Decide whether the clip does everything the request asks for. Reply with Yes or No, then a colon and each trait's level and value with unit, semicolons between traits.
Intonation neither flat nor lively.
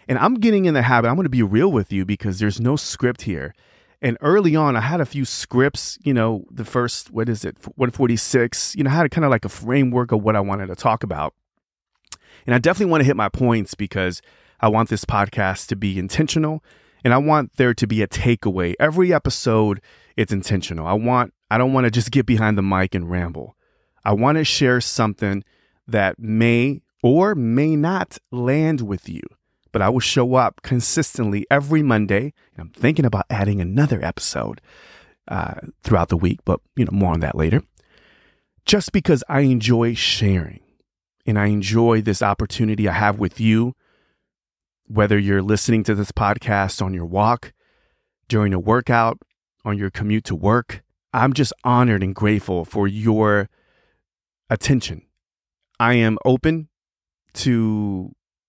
Yes: average, 4.1 semitones